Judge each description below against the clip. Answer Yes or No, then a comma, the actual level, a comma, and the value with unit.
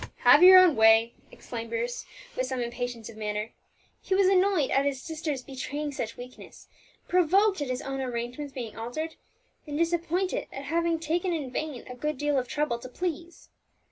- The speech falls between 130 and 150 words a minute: No, average, 175 wpm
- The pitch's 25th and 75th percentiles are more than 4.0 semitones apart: Yes, average, 5.2 semitones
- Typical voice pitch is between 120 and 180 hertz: No, very high, 280 Hz